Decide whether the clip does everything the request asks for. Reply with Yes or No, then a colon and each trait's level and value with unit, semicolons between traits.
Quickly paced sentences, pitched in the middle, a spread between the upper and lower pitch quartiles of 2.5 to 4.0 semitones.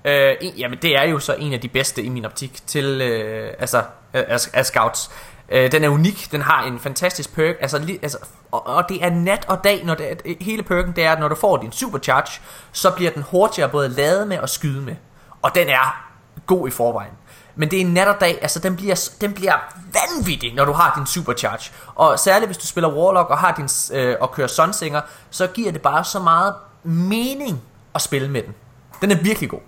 No: fast, 230 wpm; medium, 155 Hz; wide, 5.4 semitones